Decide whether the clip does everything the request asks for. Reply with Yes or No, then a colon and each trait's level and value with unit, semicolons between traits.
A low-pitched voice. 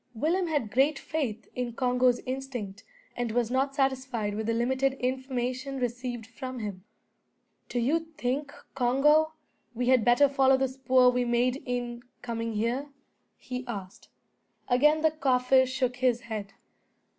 No: very high, 250 Hz